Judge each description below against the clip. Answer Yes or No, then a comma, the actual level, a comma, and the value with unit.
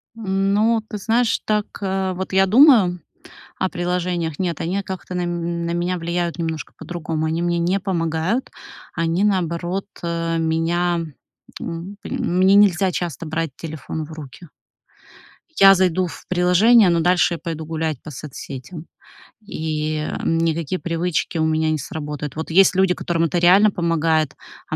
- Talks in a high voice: No, medium, 175 Hz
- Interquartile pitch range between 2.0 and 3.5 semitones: Yes, narrow, 2.6 semitones